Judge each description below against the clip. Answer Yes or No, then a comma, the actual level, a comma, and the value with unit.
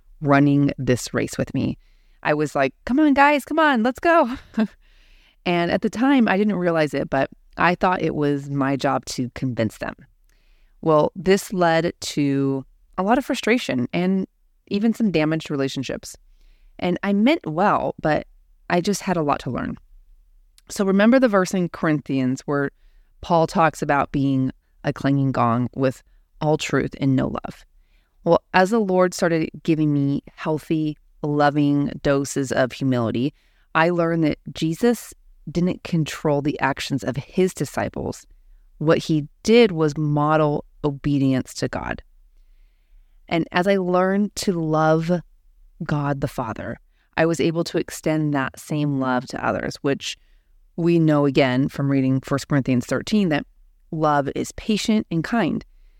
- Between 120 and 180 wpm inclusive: Yes, average, 155 wpm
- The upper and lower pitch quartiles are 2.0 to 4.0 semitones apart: No, average, 4.8 semitones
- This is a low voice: No, medium, 155 Hz